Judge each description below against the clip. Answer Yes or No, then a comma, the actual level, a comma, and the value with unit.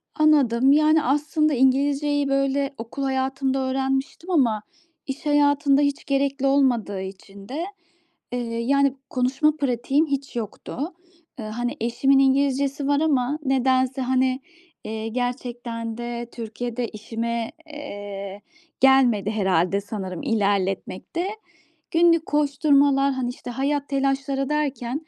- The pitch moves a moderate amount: Yes, average, 3.3 semitones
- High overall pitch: Yes, very high, 265 Hz